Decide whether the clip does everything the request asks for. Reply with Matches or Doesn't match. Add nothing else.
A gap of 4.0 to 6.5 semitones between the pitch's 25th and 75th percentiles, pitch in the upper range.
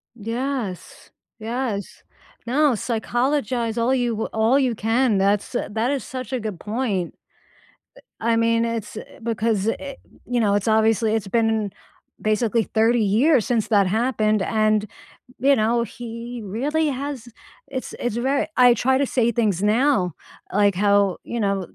Doesn't match